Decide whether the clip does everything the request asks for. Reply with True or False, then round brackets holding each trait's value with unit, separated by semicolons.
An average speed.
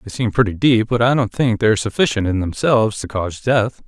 False (230 wpm)